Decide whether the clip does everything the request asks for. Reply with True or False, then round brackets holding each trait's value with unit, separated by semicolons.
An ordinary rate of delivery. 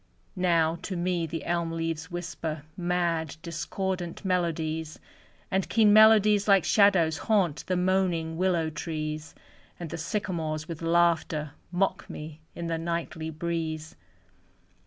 False (125 wpm)